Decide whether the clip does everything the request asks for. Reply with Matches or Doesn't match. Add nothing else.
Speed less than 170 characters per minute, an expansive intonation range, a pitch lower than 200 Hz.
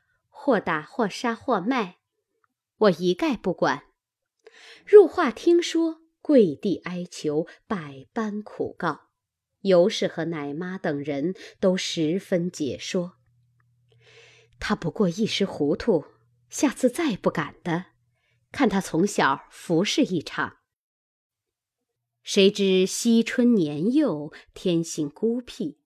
Matches